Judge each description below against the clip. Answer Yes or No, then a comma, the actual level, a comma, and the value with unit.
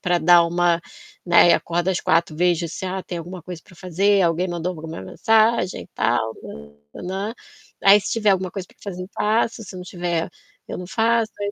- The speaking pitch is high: No, medium, 180 Hz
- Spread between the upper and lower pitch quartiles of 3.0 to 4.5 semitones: No, narrow, 2.6 semitones